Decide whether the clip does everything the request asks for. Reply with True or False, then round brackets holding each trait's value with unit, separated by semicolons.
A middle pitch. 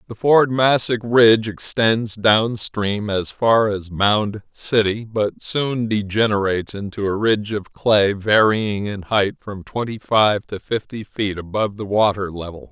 False (105 Hz)